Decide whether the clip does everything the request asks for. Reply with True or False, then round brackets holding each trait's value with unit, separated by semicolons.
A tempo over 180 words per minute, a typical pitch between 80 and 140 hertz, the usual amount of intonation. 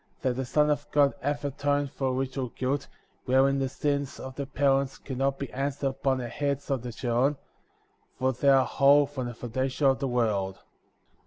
False (190 wpm; 135 Hz; 1.7 semitones)